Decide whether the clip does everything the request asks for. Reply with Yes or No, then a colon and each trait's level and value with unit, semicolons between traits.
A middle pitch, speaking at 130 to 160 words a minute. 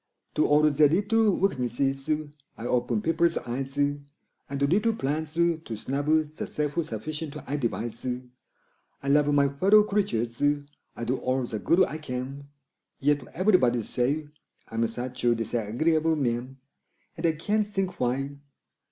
Yes: medium, 145 Hz; average, 140 wpm